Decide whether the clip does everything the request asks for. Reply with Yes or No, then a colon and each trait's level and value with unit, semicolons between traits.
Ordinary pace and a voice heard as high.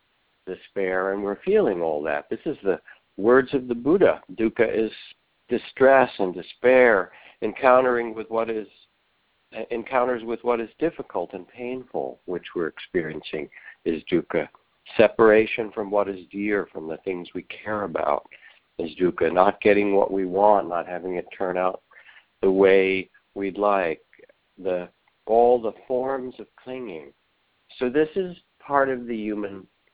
No: average, 150 wpm; low, 110 Hz